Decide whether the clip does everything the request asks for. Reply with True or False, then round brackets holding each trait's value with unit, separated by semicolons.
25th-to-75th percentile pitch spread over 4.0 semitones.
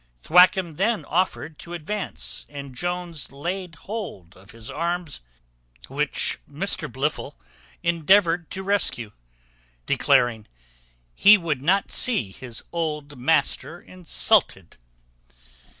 True (4.6 semitones)